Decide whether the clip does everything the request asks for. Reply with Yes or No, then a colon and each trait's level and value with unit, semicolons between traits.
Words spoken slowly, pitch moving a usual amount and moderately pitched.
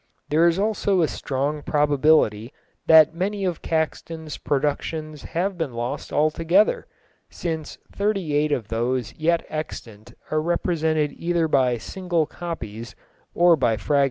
Yes: slow, 130 wpm; average, 3.5 semitones; medium, 155 Hz